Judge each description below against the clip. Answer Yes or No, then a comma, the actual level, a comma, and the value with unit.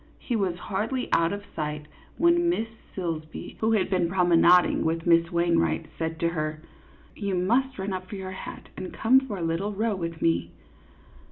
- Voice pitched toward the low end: No, medium, 180 Hz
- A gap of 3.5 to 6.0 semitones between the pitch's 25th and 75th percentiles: Yes, average, 3.8 semitones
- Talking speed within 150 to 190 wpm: Yes, average, 180 wpm